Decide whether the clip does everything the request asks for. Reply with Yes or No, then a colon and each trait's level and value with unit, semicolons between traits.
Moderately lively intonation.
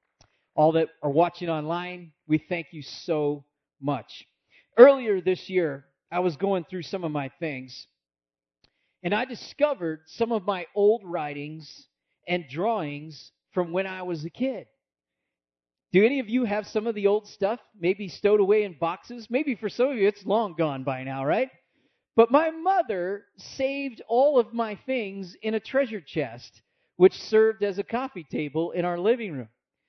No: wide, 6.0 semitones